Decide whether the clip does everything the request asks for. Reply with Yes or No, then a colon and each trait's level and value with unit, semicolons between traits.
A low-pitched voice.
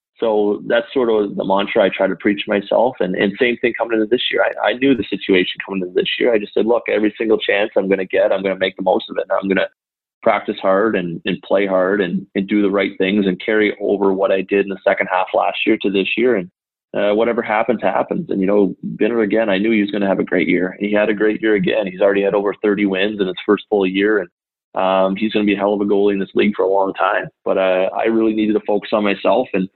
Yes: low, 100 Hz